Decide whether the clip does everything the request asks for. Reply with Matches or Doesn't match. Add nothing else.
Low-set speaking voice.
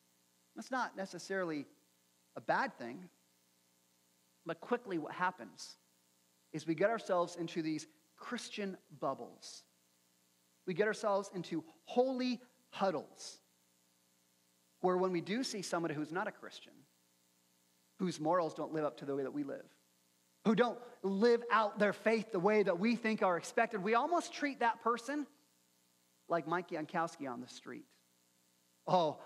Doesn't match